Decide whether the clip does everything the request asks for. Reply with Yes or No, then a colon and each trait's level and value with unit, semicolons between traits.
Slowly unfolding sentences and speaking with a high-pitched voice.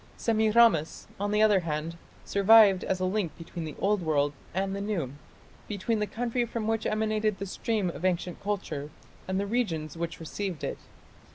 No: average, 175 wpm; high, 195 Hz